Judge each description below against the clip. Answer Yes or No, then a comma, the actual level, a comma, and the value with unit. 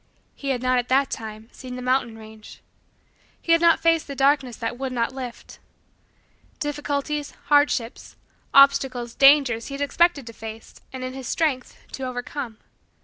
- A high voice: Yes, very high, 260 Hz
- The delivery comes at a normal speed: Yes, average, 160 wpm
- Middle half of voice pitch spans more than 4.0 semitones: No, average, 2.9 semitones